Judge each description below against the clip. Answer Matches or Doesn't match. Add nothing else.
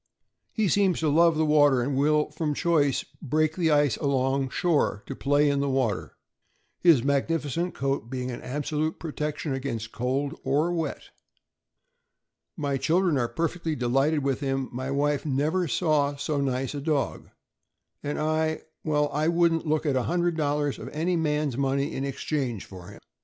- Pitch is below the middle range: Doesn't match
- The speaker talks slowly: Doesn't match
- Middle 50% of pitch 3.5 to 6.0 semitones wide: Doesn't match